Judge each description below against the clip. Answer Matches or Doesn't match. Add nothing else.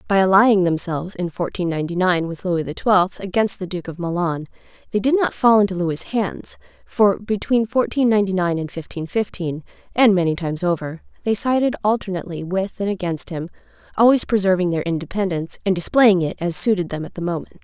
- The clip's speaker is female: Matches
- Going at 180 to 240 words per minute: Matches